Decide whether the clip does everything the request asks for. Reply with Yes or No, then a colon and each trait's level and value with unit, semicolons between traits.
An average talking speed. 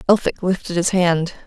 Yes: average, 165 wpm